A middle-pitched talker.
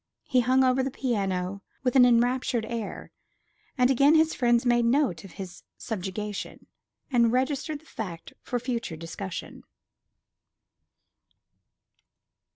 No: high, 240 Hz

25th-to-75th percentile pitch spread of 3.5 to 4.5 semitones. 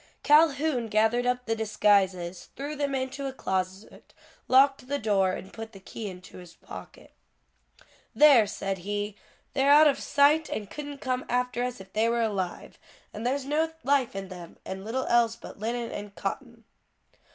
No: wide, 5.4 semitones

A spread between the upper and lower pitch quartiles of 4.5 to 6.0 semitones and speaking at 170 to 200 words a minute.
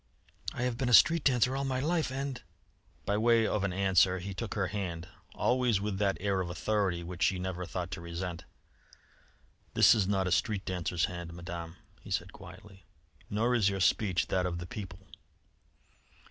No: average, 3.9 semitones; average, 190 wpm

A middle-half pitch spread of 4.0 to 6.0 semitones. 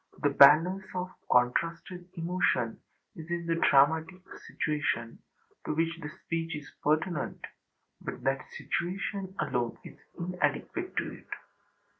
No: average, 3.6 semitones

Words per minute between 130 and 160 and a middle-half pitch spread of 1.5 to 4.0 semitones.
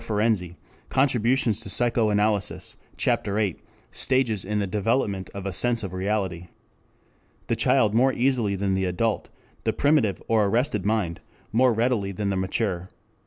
Yes: average, 145 wpm; average, 3.2 semitones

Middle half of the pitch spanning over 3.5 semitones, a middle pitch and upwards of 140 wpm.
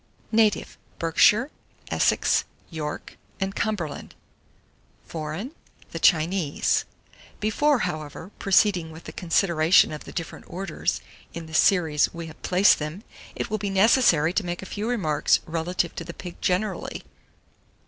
No: average, 4.0 semitones; medium, 175 Hz; slow, 135 wpm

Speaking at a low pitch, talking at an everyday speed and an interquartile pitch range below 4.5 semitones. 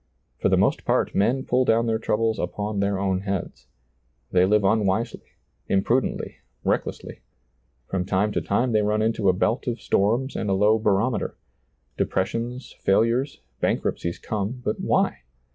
Yes: low, 105 Hz; average, 160 wpm; average, 2.9 semitones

